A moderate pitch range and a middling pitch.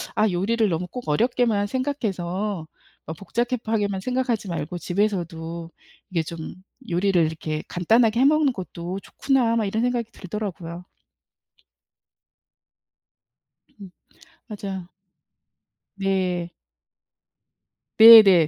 No: average, 4.7 semitones; high, 195 Hz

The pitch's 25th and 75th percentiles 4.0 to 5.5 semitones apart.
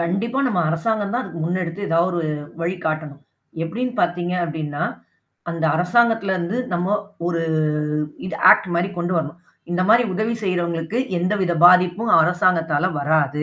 No: average, 3.1 semitones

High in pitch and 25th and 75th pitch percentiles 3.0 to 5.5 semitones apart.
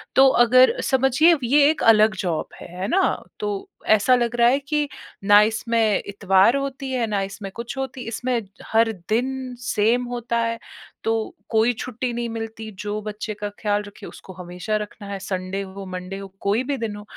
Yes: high, 225 Hz; average, 3.6 semitones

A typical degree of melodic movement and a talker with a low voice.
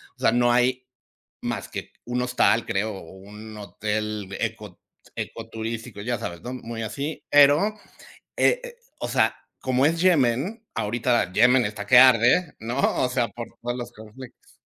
Yes: average, 3.0 semitones; low, 120 Hz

